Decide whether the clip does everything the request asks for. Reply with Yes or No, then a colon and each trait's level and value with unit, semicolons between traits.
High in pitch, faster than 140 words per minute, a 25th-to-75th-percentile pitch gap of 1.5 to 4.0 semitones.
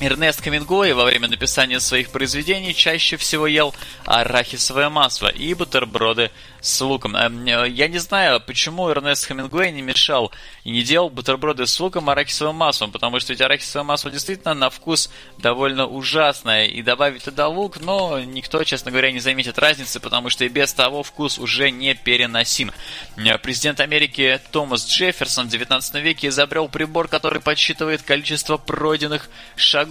No: medium, 140 Hz; average, 155 wpm; average, 3.2 semitones